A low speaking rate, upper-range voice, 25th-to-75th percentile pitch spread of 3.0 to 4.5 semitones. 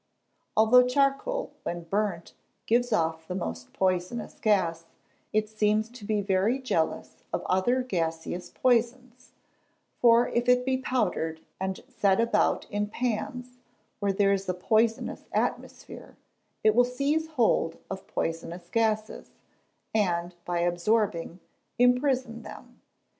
No: slow, 125 wpm; high, 215 Hz; wide, 5.4 semitones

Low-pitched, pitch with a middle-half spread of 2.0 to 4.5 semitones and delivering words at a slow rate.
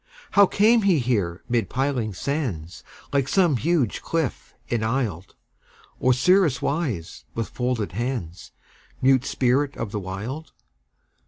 No: low, 125 Hz; average, 5.2 semitones; slow, 115 wpm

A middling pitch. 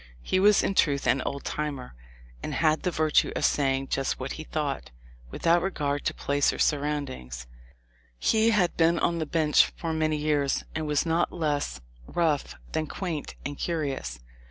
Yes: medium, 150 Hz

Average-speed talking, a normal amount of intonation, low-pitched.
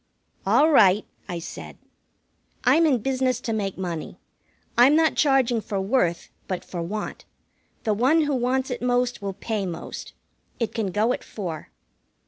No: average, 155 wpm; average, 5.0 semitones; high, 230 Hz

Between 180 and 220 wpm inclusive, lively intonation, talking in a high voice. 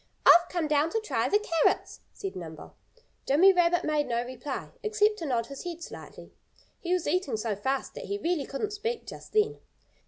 Yes: average, 190 wpm; wide, 6.6 semitones; very high, 335 Hz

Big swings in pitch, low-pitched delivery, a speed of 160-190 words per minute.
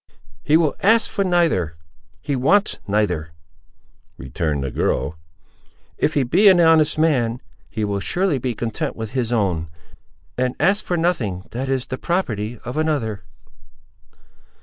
No: wide, 8.4 semitones; low, 125 Hz; average, 140 wpm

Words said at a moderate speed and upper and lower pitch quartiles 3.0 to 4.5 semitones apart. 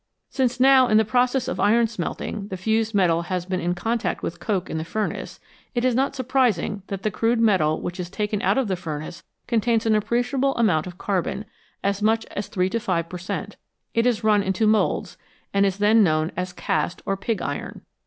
No: fast, 210 wpm; average, 4.1 semitones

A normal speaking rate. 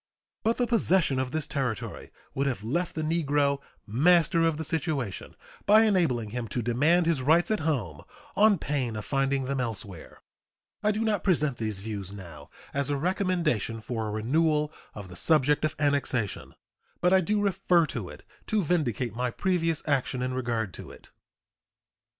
Yes: average, 170 wpm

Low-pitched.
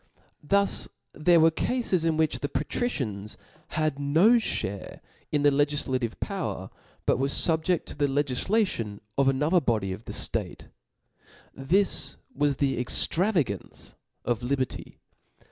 No: medium, 145 Hz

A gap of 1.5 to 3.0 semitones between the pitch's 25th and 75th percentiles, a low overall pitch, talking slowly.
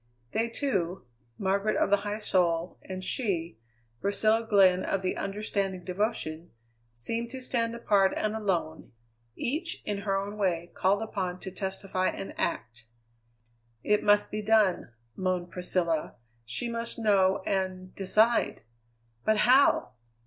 No: average, 2.7 semitones; high, 195 Hz; slow, 130 wpm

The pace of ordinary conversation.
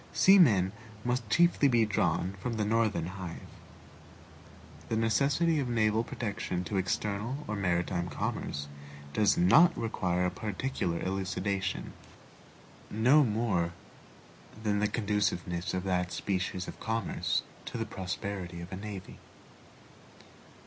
No: slow, 120 wpm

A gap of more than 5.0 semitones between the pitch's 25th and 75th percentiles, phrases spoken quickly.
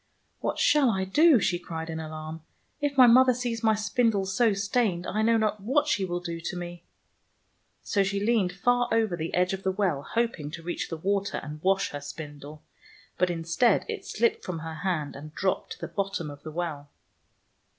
Yes: wide, 5.5 semitones; fast, 210 wpm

